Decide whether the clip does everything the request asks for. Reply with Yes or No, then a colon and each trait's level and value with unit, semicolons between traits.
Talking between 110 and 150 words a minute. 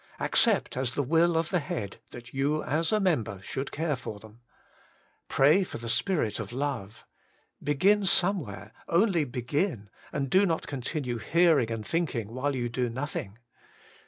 No: average, 165 wpm